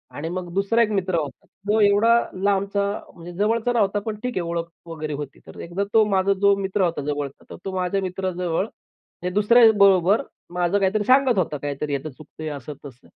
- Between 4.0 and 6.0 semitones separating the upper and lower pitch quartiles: No, average, 3.6 semitones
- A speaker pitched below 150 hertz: No, high, 190 Hz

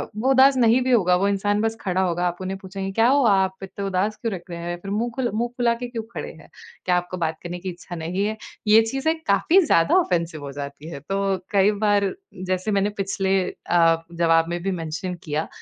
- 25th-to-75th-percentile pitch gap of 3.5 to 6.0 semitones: Yes, average, 4.2 semitones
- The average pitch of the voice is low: No, high, 195 Hz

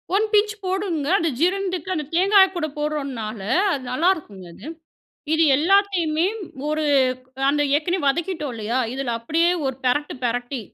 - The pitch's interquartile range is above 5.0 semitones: Yes, wide, 5.4 semitones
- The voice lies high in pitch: Yes, very high, 310 Hz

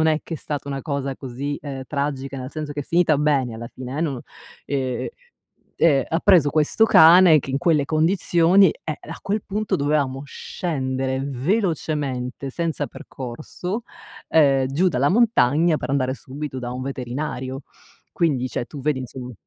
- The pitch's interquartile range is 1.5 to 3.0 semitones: No, average, 3.5 semitones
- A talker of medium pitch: Yes, medium, 145 Hz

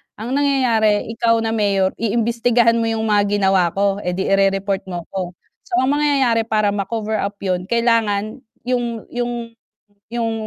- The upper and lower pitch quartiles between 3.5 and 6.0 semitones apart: No, average, 2.9 semitones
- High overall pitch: Yes, high, 220 Hz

